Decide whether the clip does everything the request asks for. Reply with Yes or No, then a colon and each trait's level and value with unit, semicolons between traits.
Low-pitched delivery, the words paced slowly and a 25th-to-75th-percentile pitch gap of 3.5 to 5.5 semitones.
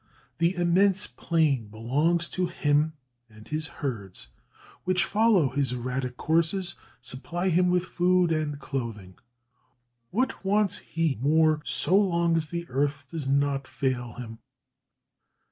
No: medium, 155 Hz; slow, 130 wpm; average, 5.1 semitones